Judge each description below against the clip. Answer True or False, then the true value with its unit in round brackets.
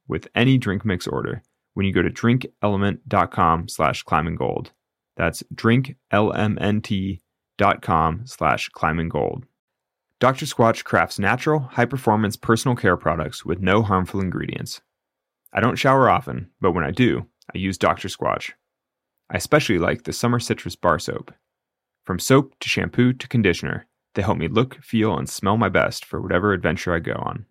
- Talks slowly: False (155 wpm)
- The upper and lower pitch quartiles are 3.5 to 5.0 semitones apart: True (4.5 semitones)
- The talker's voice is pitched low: True (110 Hz)